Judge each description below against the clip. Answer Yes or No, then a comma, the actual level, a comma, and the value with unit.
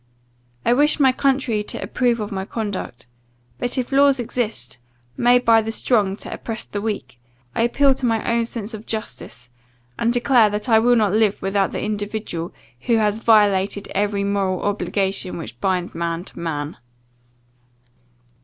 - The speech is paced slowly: No, average, 165 wpm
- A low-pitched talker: No, high, 210 Hz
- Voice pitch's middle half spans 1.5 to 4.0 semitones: Yes, average, 3.5 semitones